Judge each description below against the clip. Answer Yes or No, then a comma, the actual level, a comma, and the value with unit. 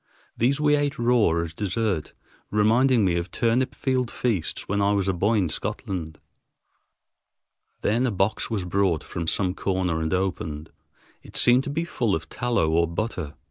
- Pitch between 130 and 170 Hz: No, low, 100 Hz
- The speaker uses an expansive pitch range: Yes, wide, 5.9 semitones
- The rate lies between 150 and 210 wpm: Yes, average, 170 wpm